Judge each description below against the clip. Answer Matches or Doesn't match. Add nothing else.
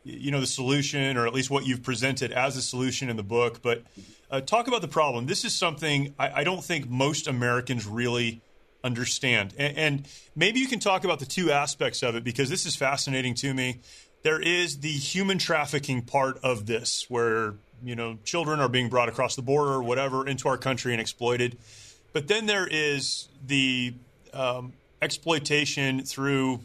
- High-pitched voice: Doesn't match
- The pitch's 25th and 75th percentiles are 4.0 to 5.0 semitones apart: Doesn't match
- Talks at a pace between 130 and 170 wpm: Doesn't match